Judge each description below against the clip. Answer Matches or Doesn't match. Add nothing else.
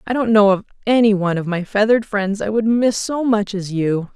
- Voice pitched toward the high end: Matches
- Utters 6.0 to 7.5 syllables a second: Doesn't match